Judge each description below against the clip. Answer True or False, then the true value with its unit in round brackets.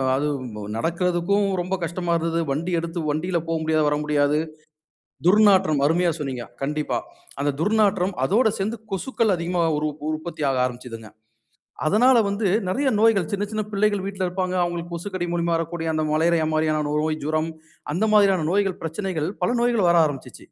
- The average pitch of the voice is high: False (170 Hz)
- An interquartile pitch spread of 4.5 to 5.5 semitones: False (3.9 semitones)